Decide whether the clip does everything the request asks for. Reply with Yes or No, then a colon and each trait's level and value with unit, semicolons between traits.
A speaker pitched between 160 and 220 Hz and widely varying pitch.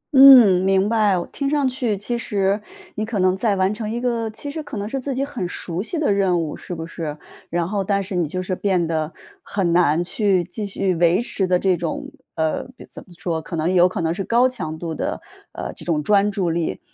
No: high, 190 Hz; average, 4.0 semitones